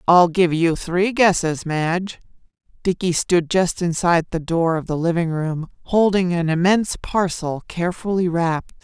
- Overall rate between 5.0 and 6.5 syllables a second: No, 4.7 syllables/s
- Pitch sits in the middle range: Yes, medium, 175 Hz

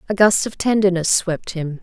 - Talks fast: No, average, 195 wpm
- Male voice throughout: No, female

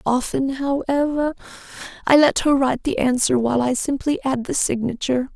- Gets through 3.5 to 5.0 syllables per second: No, 5.4 syllables/s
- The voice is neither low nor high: No, very high, 265 Hz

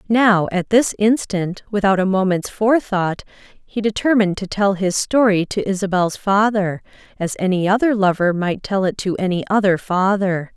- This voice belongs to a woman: Yes, female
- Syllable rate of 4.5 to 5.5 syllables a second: Yes, 4.8 syllables/s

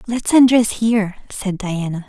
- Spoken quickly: No, average, 145 wpm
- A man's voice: No, female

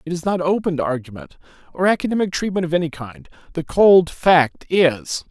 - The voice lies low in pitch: No, medium, 170 Hz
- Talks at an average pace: Yes, average, 180 wpm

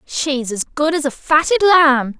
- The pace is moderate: No, fast, 220 wpm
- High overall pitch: Yes, very high, 290 Hz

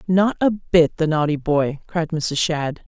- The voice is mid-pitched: Yes, medium, 160 Hz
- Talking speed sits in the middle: Yes, average, 180 wpm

